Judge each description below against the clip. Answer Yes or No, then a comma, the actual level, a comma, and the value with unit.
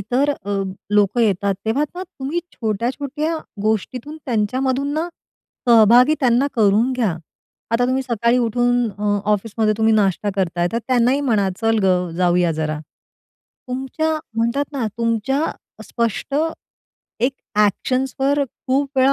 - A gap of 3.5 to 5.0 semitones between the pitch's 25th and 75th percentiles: Yes, average, 4.3 semitones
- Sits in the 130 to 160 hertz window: No, high, 235 Hz